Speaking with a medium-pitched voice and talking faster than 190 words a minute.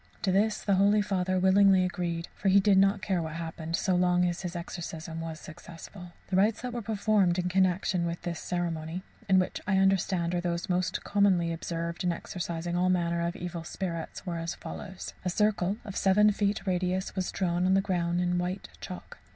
Yes: medium, 180 Hz; average, 200 wpm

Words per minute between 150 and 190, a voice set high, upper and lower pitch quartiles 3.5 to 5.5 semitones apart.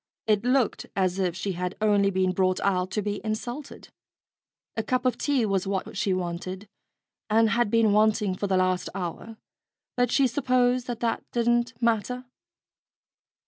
Yes: average, 160 wpm; high, 215 Hz; average, 4.1 semitones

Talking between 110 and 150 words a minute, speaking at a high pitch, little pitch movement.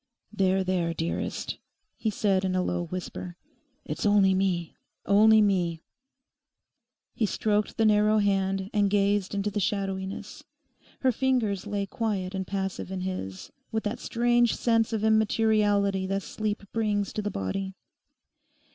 Yes: average, 140 wpm; high, 200 Hz; narrow, 2.1 semitones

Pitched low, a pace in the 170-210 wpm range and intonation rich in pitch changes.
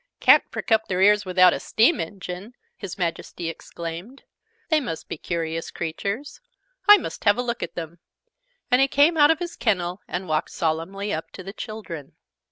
No: high, 195 Hz; average, 180 wpm; wide, 5.9 semitones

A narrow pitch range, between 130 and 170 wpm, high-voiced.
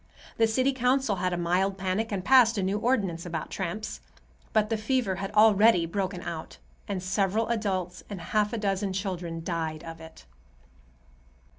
No: average, 3.5 semitones; average, 165 wpm; high, 195 Hz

